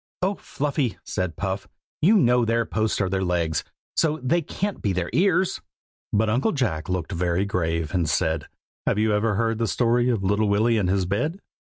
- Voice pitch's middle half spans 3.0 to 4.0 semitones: No, average, 5.1 semitones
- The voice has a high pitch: No, low, 105 Hz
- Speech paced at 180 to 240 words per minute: Yes, average, 190 wpm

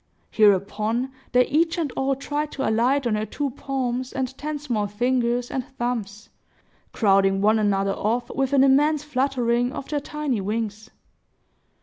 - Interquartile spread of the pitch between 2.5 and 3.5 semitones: No, average, 4.2 semitones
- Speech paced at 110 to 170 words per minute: Yes, average, 150 wpm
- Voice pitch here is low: No, high, 245 Hz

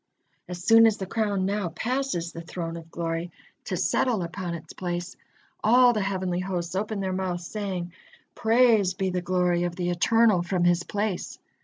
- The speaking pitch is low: No, medium, 185 Hz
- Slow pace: No, average, 175 wpm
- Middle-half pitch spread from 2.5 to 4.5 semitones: Yes, average, 3.2 semitones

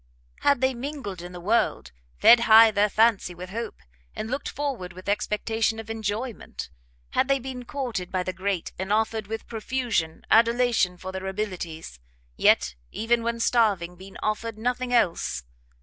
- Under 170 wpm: Yes, average, 160 wpm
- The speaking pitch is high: Yes, high, 220 Hz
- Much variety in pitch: No, average, 4.0 semitones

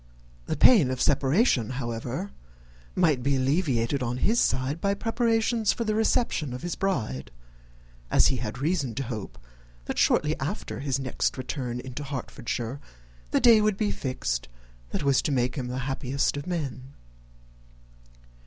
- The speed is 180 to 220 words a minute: No, average, 155 wpm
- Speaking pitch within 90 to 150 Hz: Yes, low, 135 Hz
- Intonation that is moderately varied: No, wide, 6.2 semitones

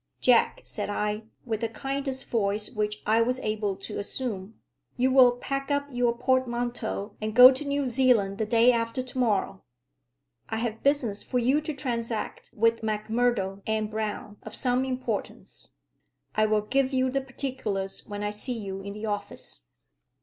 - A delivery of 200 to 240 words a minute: No, average, 165 wpm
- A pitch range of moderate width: Yes, average, 3.4 semitones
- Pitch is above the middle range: Yes, high, 230 Hz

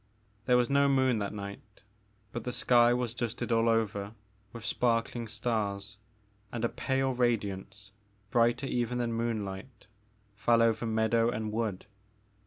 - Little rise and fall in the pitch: Yes, narrow, 2.2 semitones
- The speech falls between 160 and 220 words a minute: No, average, 140 wpm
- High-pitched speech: No, low, 115 Hz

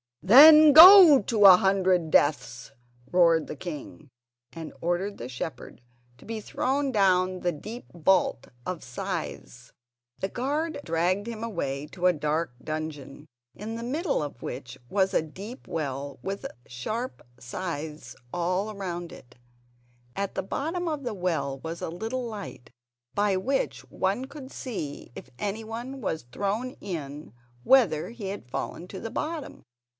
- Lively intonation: Yes, wide, 6.7 semitones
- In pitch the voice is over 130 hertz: Yes, high, 190 Hz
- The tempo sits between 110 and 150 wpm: Yes, average, 145 wpm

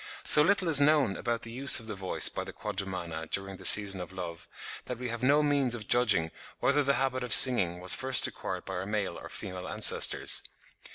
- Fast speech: Yes, fast, 215 wpm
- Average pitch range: No, wide, 5.9 semitones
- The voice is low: Yes, low, 110 Hz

